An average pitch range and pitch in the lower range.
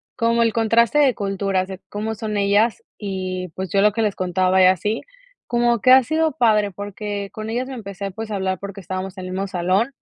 No: average, 3.2 semitones; high, 205 Hz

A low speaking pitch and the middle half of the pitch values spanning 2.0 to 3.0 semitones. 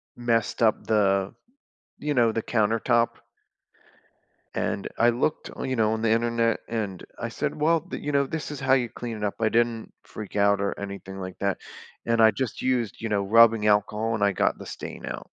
Yes: low, 115 Hz; narrow, 2.5 semitones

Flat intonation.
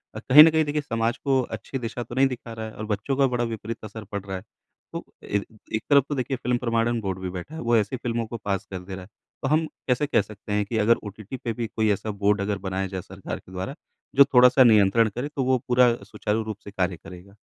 No: average, 3.7 semitones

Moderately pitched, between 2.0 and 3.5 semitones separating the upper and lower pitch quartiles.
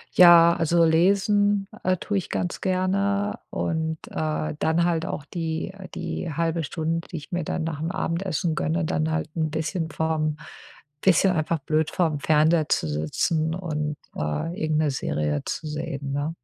Yes: medium, 160 Hz; narrow, 2.5 semitones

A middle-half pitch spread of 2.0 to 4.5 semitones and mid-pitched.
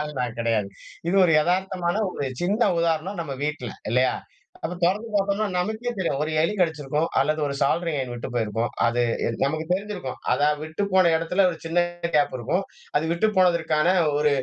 No: average, 4.9 semitones; medium, 160 Hz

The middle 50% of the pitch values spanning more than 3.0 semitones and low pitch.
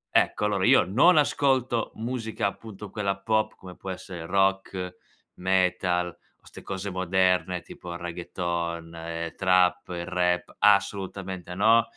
No: narrow, 2.6 semitones; very low, 95 Hz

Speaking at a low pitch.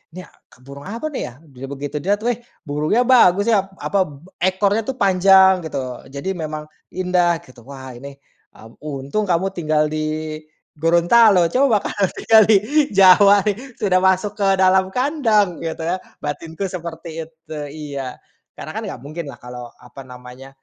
No: medium, 175 Hz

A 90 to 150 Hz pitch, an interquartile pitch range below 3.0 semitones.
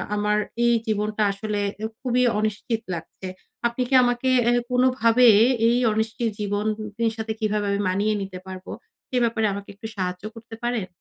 No: high, 215 Hz; narrow, 2.6 semitones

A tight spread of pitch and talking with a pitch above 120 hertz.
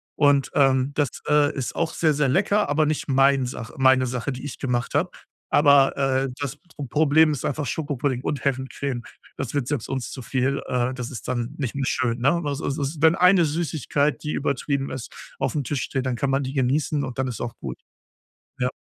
Yes: narrow, 2.3 semitones; low, 135 Hz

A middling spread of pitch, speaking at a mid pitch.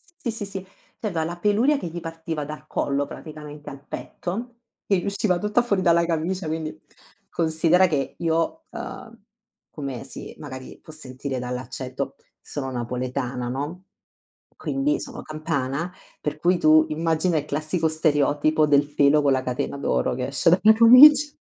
Yes: average, 4.5 semitones; medium, 155 Hz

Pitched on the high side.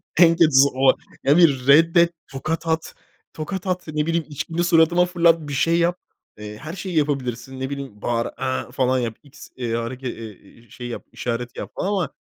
No: medium, 145 Hz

